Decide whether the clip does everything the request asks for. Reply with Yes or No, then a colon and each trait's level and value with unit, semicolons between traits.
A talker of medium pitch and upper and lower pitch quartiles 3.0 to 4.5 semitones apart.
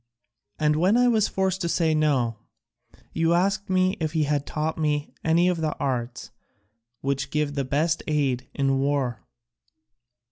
Yes: medium, 150 Hz; average, 3.6 semitones